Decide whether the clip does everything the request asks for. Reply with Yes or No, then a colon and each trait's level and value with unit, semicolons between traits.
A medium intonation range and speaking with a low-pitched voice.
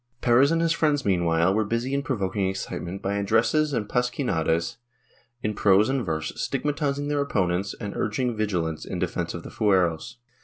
No: wide, 6.6 semitones; low, 105 Hz